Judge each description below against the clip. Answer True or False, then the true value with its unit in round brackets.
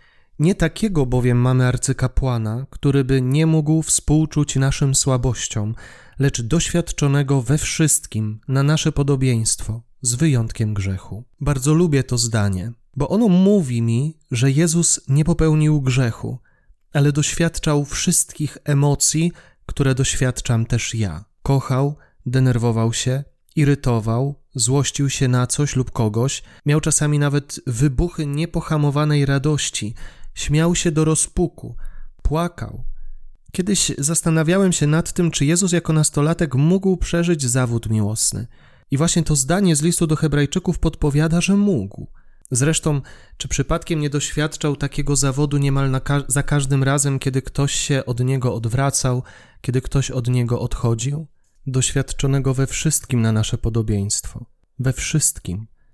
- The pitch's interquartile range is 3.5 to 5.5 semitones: True (3.9 semitones)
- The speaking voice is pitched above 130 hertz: True (140 Hz)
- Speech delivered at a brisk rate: False (130 wpm)